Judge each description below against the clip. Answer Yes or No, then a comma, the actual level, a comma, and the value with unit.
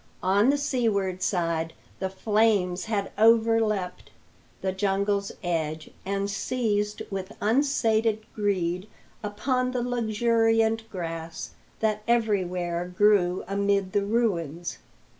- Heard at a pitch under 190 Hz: No, high, 205 Hz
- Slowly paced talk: Yes, slow, 105 wpm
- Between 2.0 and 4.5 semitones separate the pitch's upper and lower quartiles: Yes, average, 3.5 semitones